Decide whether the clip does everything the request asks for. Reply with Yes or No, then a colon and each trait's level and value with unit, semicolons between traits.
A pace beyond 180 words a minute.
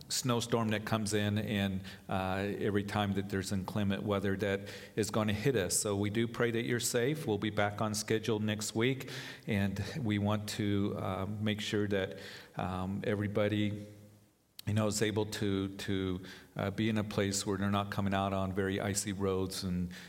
Yes: average, 200 wpm